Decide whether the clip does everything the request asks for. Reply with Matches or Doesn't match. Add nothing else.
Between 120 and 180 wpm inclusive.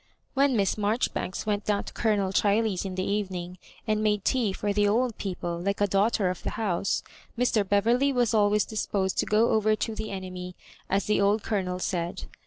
Doesn't match